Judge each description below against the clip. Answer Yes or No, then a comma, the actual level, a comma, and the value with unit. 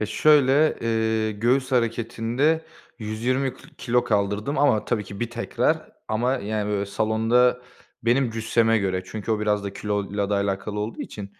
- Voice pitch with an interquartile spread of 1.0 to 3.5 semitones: Yes, average, 2.9 semitones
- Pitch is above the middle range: No, low, 110 Hz